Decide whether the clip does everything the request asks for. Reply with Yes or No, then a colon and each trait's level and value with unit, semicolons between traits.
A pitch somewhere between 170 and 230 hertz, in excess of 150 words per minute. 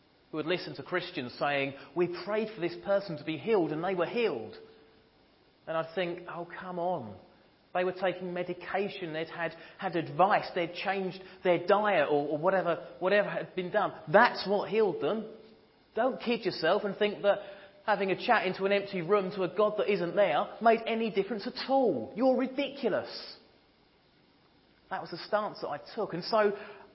Yes: high, 190 Hz; average, 185 wpm